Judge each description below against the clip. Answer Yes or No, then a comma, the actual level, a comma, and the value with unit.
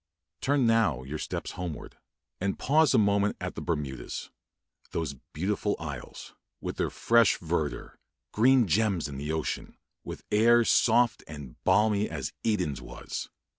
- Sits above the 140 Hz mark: No, low, 100 Hz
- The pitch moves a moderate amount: No, wide, 6.7 semitones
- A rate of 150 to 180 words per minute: No, average, 140 wpm